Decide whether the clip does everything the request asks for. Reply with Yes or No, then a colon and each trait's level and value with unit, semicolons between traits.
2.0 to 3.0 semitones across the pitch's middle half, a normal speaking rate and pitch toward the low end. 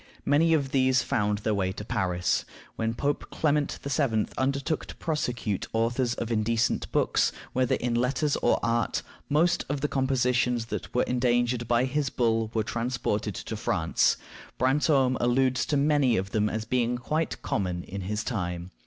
No: average, 3.5 semitones; average, 165 wpm; low, 120 Hz